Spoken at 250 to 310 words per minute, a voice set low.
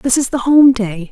No: fast, 270 wpm; high, 245 Hz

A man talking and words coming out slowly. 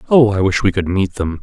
No: male; fast, 295 wpm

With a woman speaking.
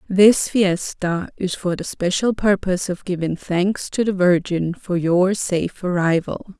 Yes: female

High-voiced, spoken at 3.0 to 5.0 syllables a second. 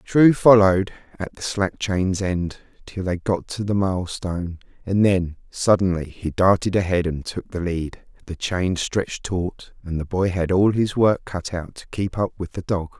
No: very low, 95 Hz; 4.5 syllables/s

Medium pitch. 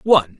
Yes: medium, 145 Hz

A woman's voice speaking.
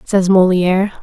Yes: female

